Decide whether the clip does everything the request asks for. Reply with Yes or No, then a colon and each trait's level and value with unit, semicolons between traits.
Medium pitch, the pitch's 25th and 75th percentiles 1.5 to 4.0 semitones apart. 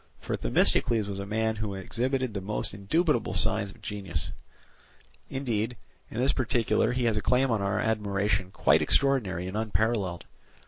No: low, 105 Hz; average, 3.4 semitones